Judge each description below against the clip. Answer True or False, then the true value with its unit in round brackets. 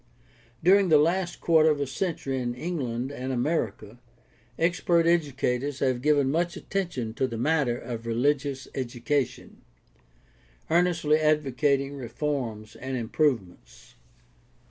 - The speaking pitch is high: False (140 Hz)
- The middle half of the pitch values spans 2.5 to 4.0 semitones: False (4.4 semitones)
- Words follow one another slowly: True (115 wpm)